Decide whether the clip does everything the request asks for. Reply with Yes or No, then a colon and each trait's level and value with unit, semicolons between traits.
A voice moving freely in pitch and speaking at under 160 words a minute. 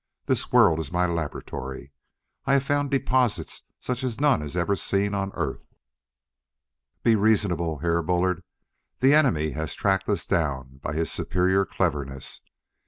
Yes: wide, 6.1 semitones; average, 145 wpm